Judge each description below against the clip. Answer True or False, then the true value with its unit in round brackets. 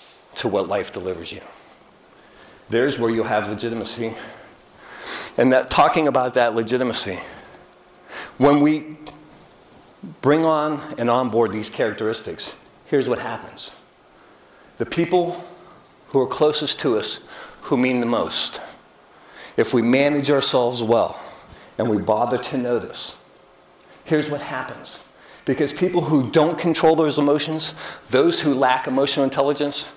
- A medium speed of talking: False (125 wpm)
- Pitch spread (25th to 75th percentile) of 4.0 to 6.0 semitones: True (4.3 semitones)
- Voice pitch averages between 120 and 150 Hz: True (140 Hz)